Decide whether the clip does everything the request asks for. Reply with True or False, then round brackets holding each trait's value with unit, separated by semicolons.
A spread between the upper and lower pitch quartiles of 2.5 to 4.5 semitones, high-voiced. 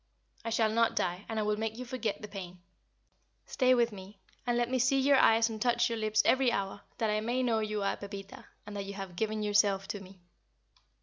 True (2.9 semitones; 215 Hz)